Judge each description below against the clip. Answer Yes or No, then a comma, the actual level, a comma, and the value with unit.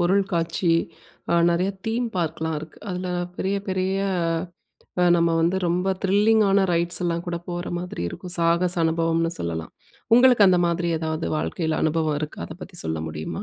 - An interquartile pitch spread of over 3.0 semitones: No, narrow, 2.4 semitones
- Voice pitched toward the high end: No, medium, 170 Hz